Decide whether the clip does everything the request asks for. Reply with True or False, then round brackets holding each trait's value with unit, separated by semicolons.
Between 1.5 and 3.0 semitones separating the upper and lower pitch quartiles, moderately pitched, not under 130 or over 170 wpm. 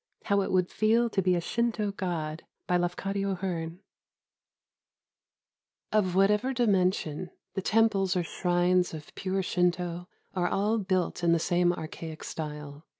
True (2.4 semitones; 180 Hz; 140 wpm)